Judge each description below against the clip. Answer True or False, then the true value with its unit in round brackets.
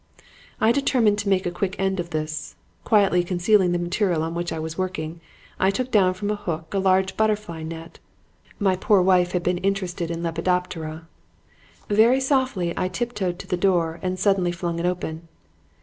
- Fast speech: False (180 wpm)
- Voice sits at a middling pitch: True (180 Hz)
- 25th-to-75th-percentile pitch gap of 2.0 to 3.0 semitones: True (2.7 semitones)